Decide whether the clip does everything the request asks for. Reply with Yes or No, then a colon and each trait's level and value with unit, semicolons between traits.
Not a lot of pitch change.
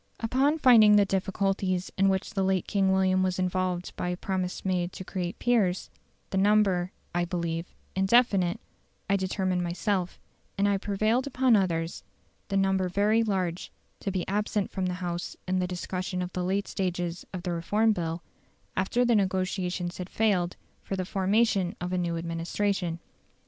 Yes: narrow, 2.0 semitones